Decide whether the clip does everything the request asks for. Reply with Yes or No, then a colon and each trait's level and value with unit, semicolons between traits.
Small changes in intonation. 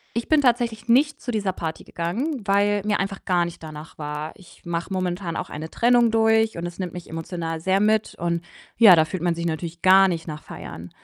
No: average, 4.6 semitones